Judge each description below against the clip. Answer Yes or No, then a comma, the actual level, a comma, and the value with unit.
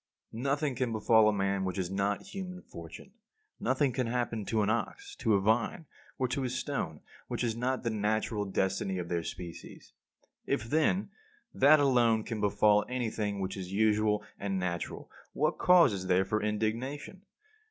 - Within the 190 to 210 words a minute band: No, average, 175 wpm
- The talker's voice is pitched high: No, low, 110 Hz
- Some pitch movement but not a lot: Yes, average, 4.7 semitones